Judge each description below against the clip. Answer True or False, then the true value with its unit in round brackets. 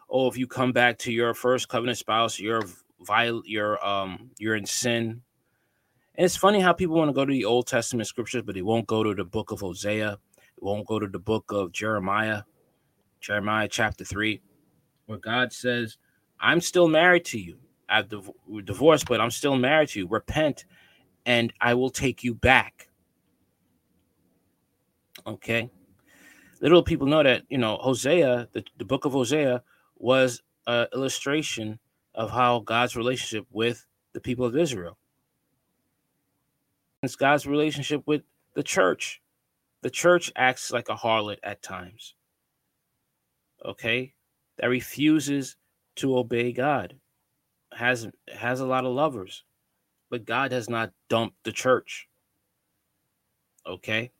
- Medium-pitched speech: False (120 Hz)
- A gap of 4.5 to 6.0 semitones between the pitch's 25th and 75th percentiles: False (3.6 semitones)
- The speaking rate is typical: True (145 wpm)